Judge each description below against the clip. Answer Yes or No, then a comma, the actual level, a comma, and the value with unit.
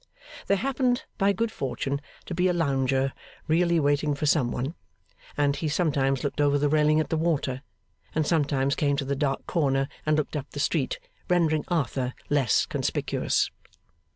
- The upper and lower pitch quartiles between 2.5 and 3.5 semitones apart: Yes, average, 3.2 semitones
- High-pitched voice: No, medium, 145 Hz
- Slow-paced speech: No, average, 170 wpm